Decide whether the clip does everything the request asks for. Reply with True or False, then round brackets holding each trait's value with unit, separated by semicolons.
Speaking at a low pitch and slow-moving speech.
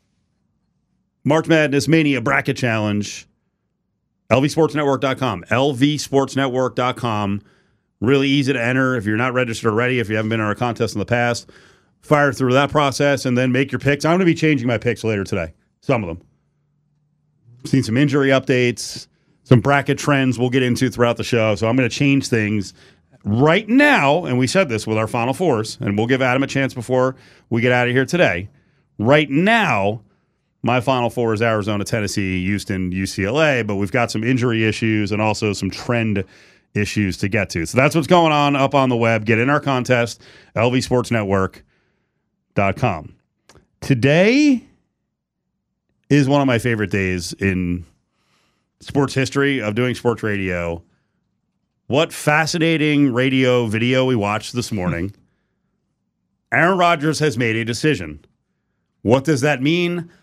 False (125 Hz; 160 wpm)